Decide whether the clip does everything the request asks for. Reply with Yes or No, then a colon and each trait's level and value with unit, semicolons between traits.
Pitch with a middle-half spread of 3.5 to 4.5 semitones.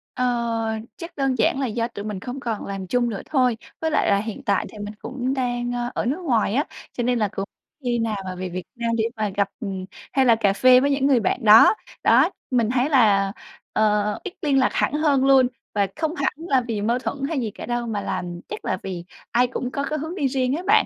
Yes: average, 4.1 semitones